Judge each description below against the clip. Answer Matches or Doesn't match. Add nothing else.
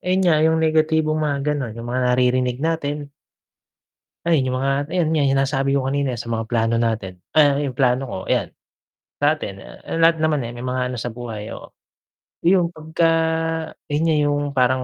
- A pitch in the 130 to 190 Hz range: Matches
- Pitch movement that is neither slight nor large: Matches